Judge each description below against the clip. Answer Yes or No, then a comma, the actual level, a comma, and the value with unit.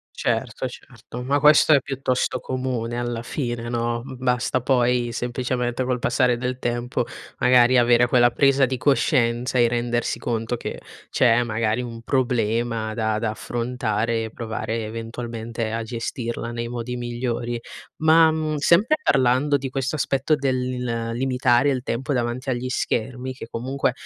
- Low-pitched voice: Yes, low, 120 Hz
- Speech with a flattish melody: Yes, narrow, 1.7 semitones